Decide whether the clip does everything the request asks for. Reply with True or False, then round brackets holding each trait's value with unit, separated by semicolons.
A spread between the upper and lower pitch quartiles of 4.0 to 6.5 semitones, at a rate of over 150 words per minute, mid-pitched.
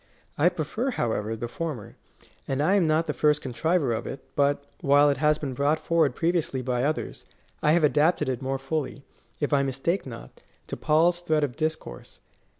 False (3.2 semitones; 190 wpm; 145 Hz)